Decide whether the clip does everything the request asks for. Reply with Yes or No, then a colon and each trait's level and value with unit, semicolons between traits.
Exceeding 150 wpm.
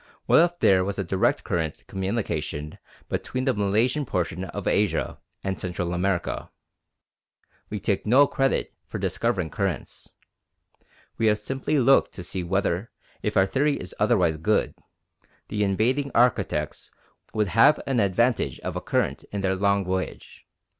No: average, 145 wpm